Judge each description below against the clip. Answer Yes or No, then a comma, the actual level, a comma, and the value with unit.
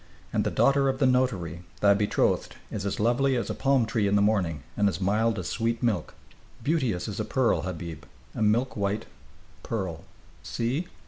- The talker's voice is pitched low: Yes, low, 110 Hz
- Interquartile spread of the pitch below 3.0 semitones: No, average, 4.3 semitones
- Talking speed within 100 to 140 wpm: No, average, 185 wpm